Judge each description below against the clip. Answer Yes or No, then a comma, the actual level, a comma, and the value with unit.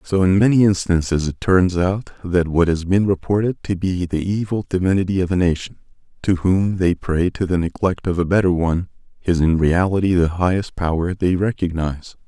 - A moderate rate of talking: Yes, average, 190 wpm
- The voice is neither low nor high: No, very low, 90 Hz